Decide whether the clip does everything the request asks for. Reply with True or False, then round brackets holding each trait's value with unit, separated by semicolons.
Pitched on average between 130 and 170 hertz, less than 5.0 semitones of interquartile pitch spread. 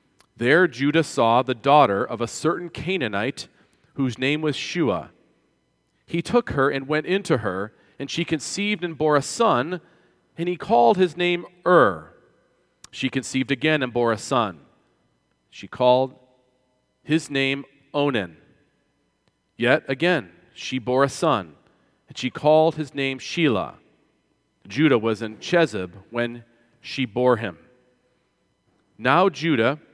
True (140 Hz; 4.4 semitones)